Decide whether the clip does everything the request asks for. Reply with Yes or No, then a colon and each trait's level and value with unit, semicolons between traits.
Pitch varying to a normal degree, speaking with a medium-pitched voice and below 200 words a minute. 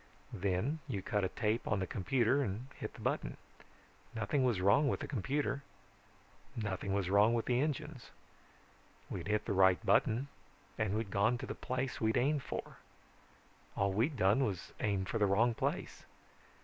No: average, 4.6 semitones; low, 110 Hz; average, 170 wpm